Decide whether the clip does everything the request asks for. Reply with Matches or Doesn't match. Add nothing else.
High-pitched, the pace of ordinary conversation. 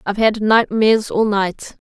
Matches